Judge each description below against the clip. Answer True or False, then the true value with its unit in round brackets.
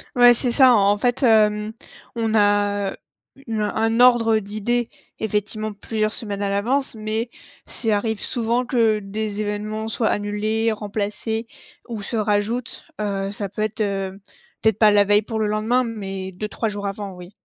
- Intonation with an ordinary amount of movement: False (1.7 semitones)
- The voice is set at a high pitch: True (215 Hz)